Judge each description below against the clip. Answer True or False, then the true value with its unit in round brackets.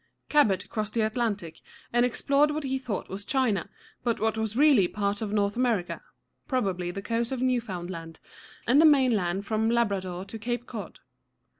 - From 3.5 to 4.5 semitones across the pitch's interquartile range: True (4.0 semitones)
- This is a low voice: False (220 Hz)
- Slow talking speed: False (175 wpm)